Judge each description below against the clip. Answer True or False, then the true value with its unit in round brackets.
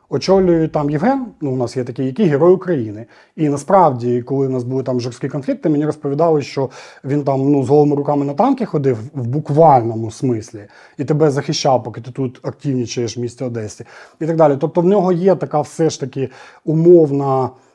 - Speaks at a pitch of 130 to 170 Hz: True (140 Hz)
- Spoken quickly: True (195 wpm)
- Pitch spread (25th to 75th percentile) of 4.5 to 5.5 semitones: False (3.7 semitones)